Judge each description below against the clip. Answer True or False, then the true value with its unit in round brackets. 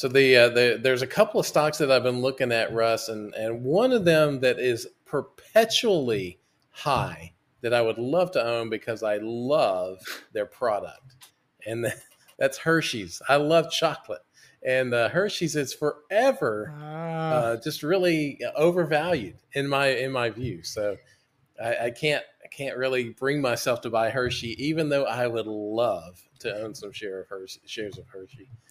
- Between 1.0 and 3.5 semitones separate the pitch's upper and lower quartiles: False (5.0 semitones)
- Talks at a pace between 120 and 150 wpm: False (170 wpm)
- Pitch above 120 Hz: True (135 Hz)